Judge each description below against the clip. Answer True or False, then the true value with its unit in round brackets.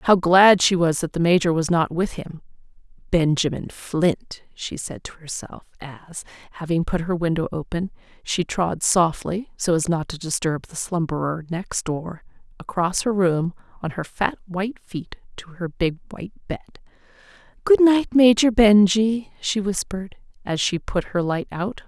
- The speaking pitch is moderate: True (180 Hz)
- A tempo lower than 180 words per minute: True (165 wpm)